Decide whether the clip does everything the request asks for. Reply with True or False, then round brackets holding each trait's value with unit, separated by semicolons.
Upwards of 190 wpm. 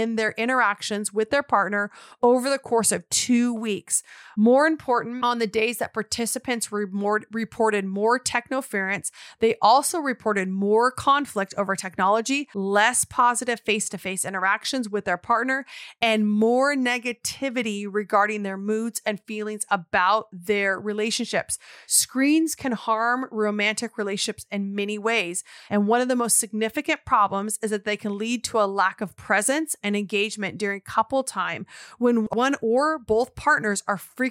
False (150 wpm)